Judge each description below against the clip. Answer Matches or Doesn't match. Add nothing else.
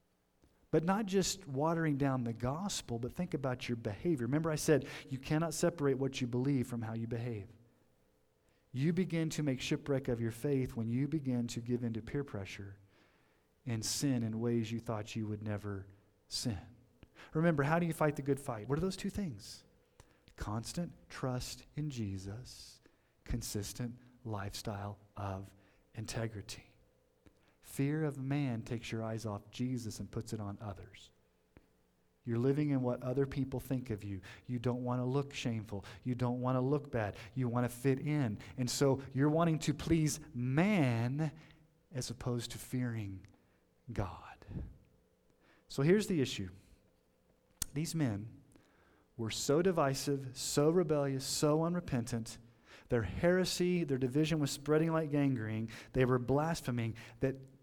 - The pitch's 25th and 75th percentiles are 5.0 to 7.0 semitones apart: Doesn't match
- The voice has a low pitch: Matches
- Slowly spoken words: Doesn't match